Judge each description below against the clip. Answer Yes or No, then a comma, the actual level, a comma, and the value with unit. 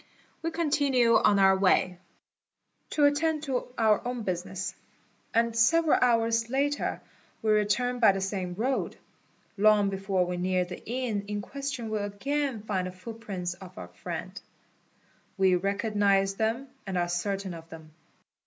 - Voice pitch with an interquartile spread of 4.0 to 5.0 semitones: Yes, average, 4.5 semitones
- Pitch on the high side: Yes, high, 210 Hz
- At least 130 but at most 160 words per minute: Yes, average, 145 wpm